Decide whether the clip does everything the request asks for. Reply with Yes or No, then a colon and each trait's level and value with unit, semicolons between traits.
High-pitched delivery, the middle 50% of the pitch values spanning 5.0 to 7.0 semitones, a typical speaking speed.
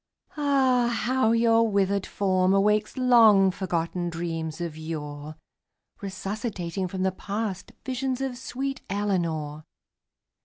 No: high, 195 Hz; average, 5.3 semitones; slow, 110 wpm